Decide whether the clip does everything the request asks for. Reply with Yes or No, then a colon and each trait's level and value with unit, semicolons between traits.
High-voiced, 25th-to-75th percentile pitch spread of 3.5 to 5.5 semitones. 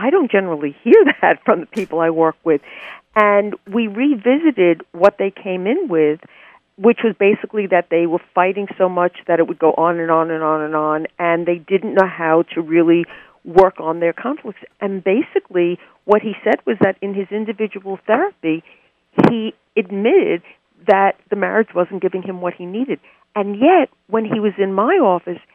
Yes: high, 195 Hz; average, 4.1 semitones